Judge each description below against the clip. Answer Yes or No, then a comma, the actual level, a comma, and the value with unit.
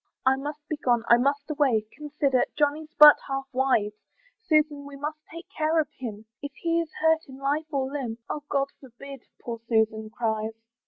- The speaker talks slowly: No, average, 180 wpm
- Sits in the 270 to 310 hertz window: Yes, very high, 275 Hz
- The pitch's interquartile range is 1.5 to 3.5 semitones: No, average, 3.9 semitones